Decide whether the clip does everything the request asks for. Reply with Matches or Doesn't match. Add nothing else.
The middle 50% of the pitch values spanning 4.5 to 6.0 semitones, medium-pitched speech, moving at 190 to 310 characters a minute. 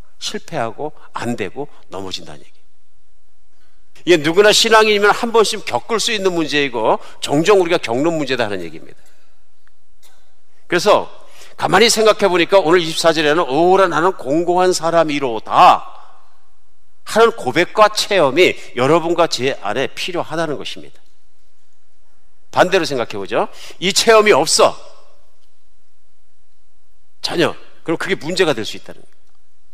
Matches